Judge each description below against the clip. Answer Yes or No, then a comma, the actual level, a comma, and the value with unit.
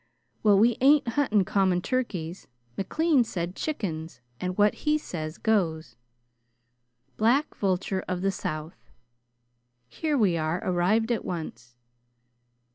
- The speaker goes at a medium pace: No, slow, 120 wpm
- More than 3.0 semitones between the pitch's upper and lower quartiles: Yes, wide, 5.5 semitones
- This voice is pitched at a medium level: No, high, 195 Hz